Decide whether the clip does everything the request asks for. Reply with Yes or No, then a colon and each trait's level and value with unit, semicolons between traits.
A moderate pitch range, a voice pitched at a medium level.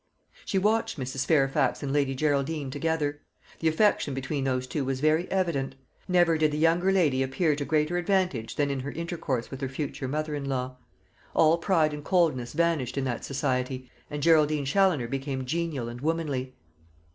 Yes: average, 3.5 semitones; medium, 145 Hz